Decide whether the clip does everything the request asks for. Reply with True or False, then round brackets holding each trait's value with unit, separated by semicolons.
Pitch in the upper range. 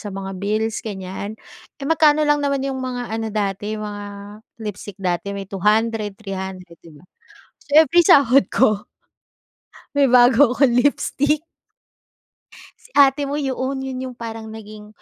True (225 Hz)